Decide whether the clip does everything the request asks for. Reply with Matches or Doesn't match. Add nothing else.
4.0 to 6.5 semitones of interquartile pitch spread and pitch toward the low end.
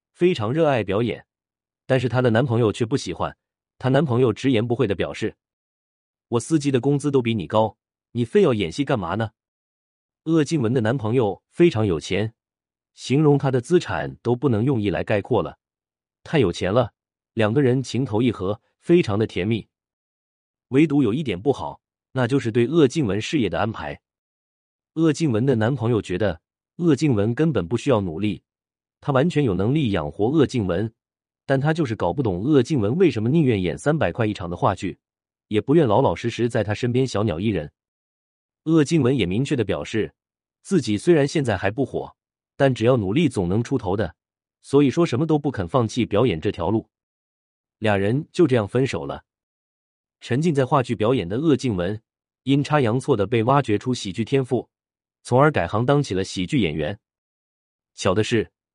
Matches